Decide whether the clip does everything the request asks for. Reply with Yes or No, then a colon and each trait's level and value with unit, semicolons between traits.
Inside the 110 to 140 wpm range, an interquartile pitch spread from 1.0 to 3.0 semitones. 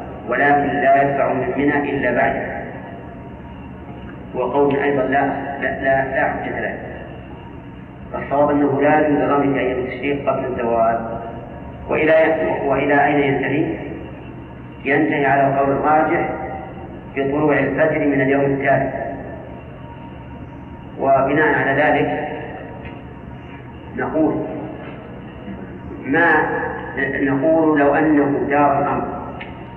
No: average, 90 wpm; narrow, 2.4 semitones